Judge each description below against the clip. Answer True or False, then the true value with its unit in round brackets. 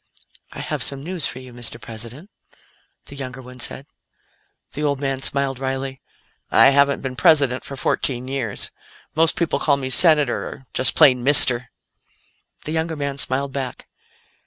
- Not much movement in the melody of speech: True (2.0 semitones)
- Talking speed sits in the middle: True (160 wpm)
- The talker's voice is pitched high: False (135 Hz)